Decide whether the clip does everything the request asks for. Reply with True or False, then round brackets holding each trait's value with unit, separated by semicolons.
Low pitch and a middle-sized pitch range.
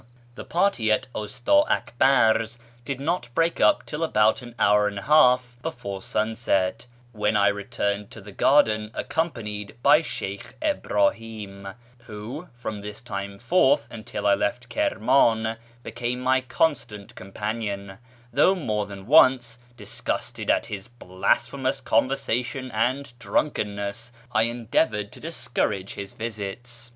True (115 Hz; 3.9 semitones)